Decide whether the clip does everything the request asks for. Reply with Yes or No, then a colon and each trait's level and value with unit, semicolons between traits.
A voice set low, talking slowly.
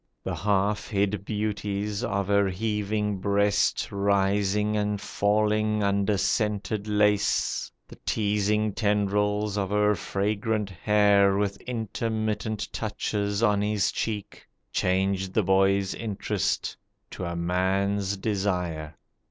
Yes: low, 100 Hz; slow, 110 wpm